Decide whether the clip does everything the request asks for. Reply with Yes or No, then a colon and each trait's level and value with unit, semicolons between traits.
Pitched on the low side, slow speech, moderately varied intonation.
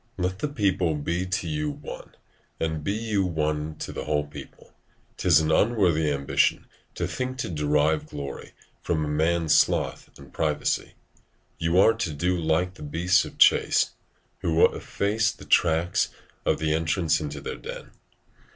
No: very low, 80 Hz; average, 160 wpm; average, 3.6 semitones